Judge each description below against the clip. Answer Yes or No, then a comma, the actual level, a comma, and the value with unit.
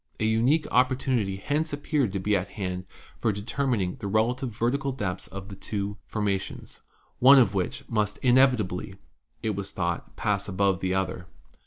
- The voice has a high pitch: No, low, 105 Hz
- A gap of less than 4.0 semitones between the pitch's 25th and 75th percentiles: No, average, 4.7 semitones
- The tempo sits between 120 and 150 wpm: No, average, 170 wpm